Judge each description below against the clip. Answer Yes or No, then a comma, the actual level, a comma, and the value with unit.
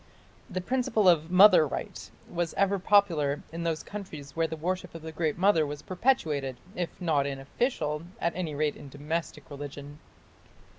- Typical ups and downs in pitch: Yes, average, 3.9 semitones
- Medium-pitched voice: Yes, medium, 165 Hz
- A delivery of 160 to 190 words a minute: Yes, average, 165 wpm